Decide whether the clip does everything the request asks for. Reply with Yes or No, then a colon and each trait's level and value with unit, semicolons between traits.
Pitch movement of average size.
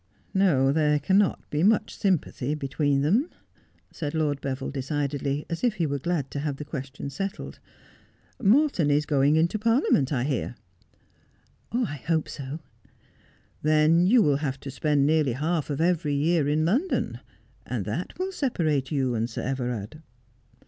Yes: average, 3.8 semitones